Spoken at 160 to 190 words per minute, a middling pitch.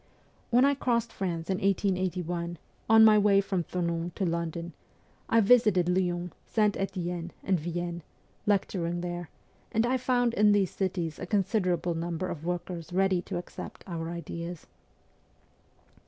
No: average, 140 wpm; medium, 180 Hz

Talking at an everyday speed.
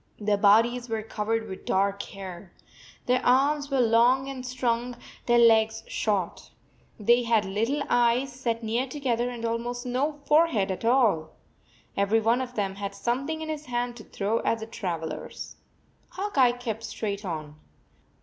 Yes: average, 160 wpm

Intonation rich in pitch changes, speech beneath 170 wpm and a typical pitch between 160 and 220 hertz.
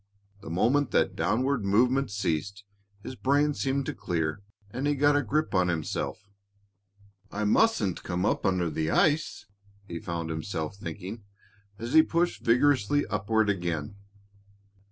No: wide, 7.8 semitones; average, 140 wpm; low, 105 Hz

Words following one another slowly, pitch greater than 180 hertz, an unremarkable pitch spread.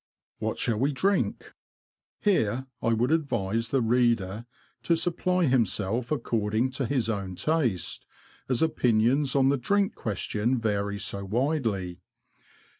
No: slow, 125 wpm; low, 120 Hz; average, 4.7 semitones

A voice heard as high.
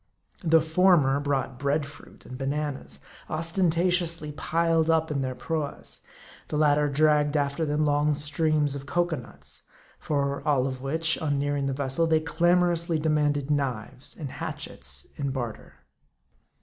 No: medium, 150 Hz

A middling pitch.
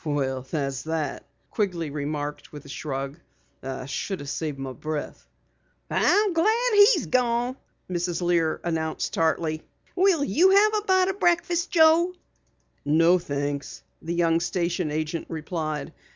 Yes: medium, 165 Hz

